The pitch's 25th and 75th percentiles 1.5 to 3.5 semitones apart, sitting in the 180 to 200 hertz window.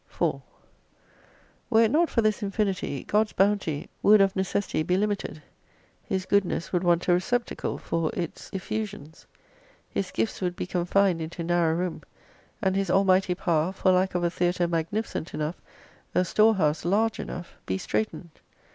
Yes: average, 3.0 semitones; medium, 185 Hz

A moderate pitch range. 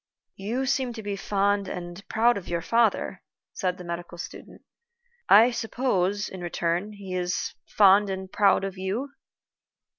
Yes: average, 3.2 semitones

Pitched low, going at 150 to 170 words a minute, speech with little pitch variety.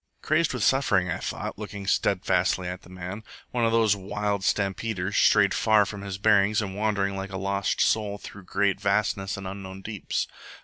No: low, 100 Hz; average, 180 wpm; narrow, 1.7 semitones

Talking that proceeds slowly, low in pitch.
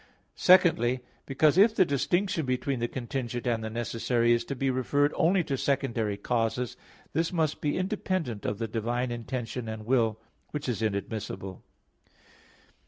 No: average, 150 wpm; low, 125 Hz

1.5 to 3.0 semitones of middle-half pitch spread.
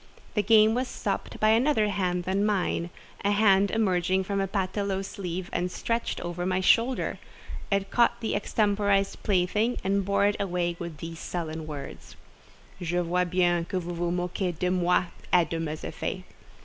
Yes: narrow, 2.6 semitones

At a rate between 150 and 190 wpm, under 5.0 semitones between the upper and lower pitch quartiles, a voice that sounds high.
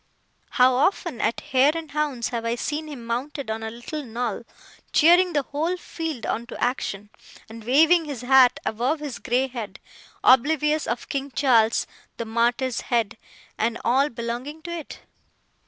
Yes: average, 160 wpm; average, 4.4 semitones; very high, 255 Hz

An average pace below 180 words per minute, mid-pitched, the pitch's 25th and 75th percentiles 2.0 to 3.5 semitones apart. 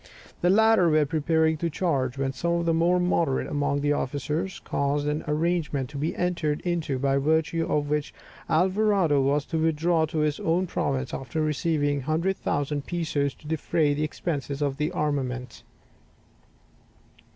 Yes: average, 155 wpm; medium, 150 Hz; average, 2.8 semitones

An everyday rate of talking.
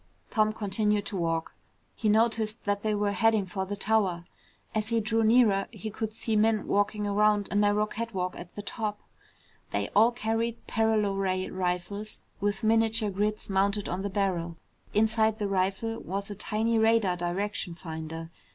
Yes: average, 165 wpm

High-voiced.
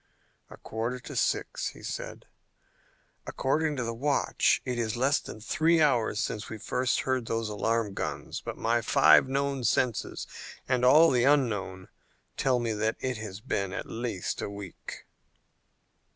No: low, 120 Hz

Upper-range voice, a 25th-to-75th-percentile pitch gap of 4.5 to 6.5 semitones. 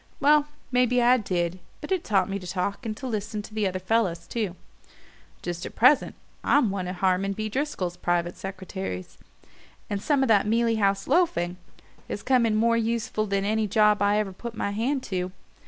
No: high, 210 Hz; average, 3.6 semitones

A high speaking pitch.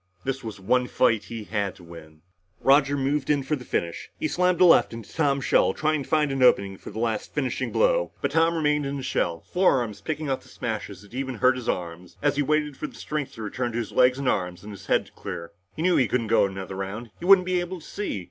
No: low, 130 Hz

